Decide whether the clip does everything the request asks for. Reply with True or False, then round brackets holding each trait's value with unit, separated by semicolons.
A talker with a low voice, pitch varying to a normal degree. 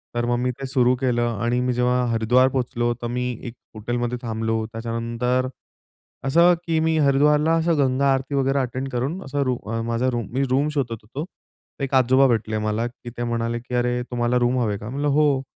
False (125 Hz; 2.3 semitones)